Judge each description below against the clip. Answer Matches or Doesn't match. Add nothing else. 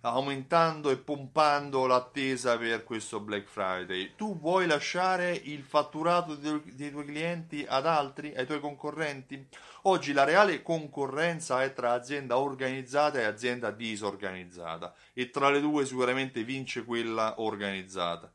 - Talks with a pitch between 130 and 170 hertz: Matches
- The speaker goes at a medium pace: Matches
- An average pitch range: Matches